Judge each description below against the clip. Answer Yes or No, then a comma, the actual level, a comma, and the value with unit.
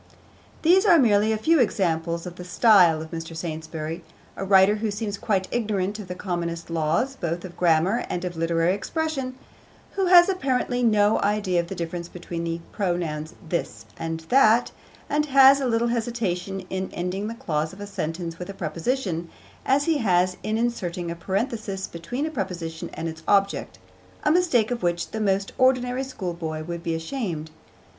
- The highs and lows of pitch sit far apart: Yes, wide, 5.8 semitones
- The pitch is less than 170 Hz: No, high, 190 Hz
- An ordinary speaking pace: Yes, average, 175 wpm